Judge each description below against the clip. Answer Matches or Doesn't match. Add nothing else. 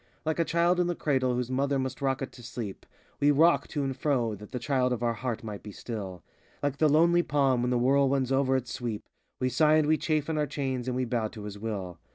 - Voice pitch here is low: Matches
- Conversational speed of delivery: Doesn't match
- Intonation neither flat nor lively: Matches